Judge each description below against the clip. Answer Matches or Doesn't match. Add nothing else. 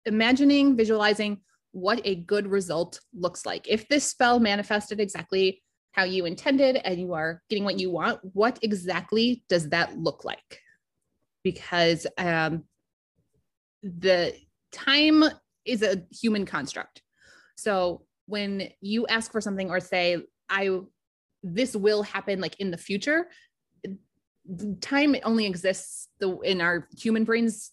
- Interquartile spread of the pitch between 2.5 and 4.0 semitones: Matches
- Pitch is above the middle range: Matches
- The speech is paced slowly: Matches